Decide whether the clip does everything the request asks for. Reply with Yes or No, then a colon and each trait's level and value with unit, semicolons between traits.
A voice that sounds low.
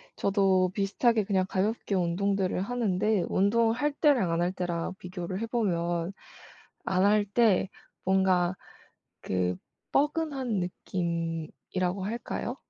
No: high, 190 Hz